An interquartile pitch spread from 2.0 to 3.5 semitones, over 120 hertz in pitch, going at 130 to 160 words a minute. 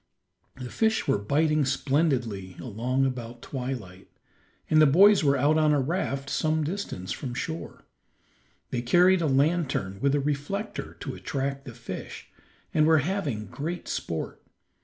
No: average, 4.2 semitones; medium, 140 Hz; average, 145 wpm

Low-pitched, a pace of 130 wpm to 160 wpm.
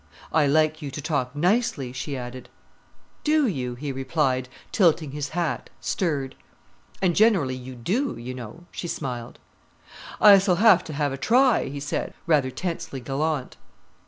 No: medium, 145 Hz; average, 155 wpm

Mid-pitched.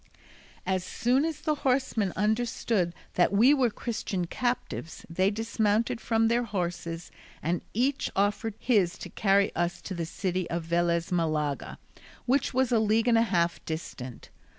No: high, 205 Hz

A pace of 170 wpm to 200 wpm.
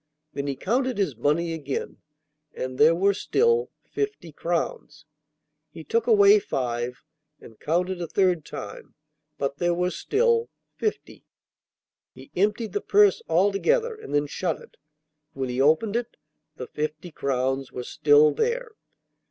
No: average, 140 wpm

